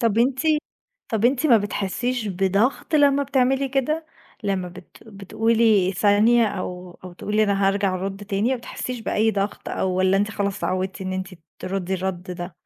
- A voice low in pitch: No, high, 205 Hz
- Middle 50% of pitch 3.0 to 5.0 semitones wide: Yes, average, 4.0 semitones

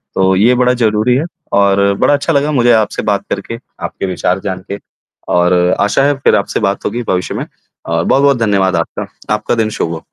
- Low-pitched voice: Yes, low, 105 Hz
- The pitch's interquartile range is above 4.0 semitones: Yes, average, 4.6 semitones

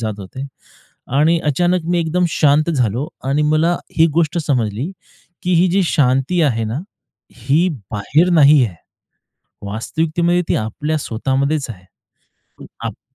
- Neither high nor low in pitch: Yes, medium, 150 Hz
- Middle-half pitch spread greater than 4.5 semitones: Yes, average, 5.2 semitones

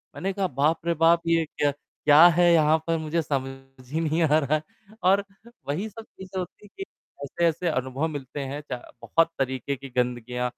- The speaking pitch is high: No, medium, 155 Hz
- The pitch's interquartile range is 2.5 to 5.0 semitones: Yes, average, 3.9 semitones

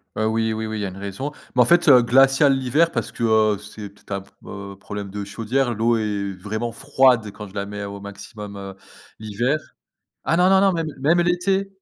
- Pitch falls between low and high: No, low, 110 Hz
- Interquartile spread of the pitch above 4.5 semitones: Yes, average, 5.1 semitones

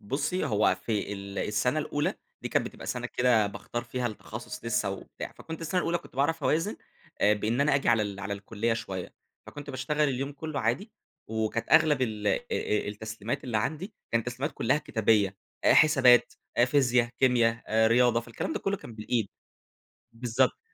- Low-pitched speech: Yes, low, 120 Hz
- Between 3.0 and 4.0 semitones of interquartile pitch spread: No, average, 4.7 semitones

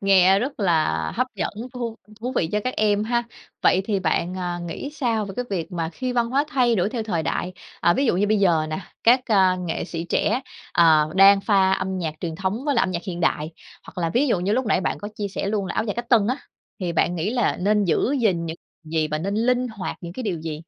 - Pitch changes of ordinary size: Yes, average, 5.0 semitones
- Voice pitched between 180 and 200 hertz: Yes, high, 195 Hz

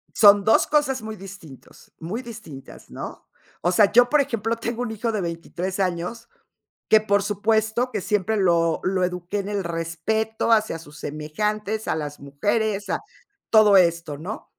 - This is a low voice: No, high, 200 Hz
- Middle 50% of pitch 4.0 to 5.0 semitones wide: Yes, average, 4.5 semitones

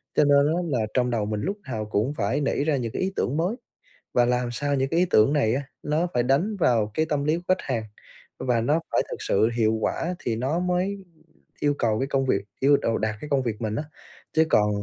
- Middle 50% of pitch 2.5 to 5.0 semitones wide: No, wide, 5.4 semitones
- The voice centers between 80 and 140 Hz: Yes, low, 135 Hz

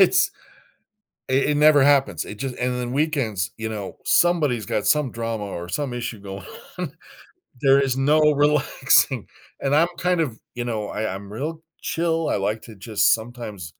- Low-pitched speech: Yes, low, 125 Hz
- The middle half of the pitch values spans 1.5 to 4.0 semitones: No, wide, 5.4 semitones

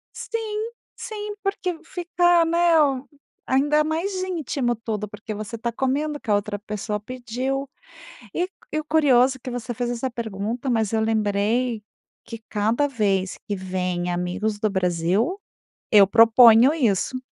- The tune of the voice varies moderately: No, wide, 6.1 semitones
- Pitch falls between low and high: No, high, 240 Hz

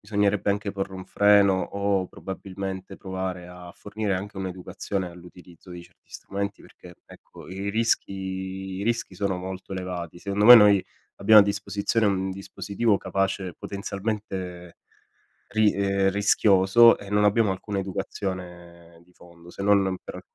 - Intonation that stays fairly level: Yes, narrow, 1.6 semitones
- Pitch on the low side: Yes, very low, 95 Hz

